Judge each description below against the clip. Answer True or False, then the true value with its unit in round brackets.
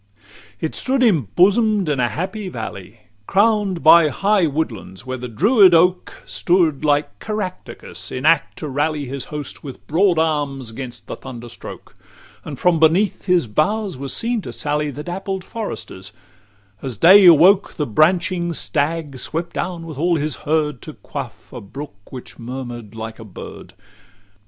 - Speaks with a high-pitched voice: False (155 Hz)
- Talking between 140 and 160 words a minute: True (155 wpm)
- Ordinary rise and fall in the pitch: False (5.9 semitones)